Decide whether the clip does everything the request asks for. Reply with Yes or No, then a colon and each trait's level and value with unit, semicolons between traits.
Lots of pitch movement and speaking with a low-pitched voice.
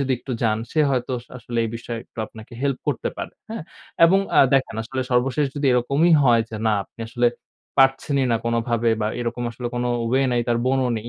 No: narrow, 2.4 semitones; low, 125 Hz